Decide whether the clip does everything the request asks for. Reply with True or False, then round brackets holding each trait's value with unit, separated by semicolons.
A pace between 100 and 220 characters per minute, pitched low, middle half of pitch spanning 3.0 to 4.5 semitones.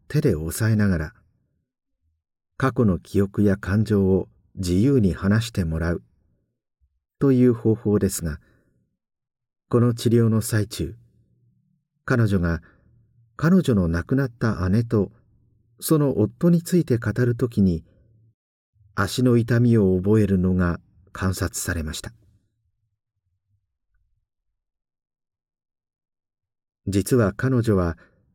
True (185 characters per minute; 105 Hz; 4.2 semitones)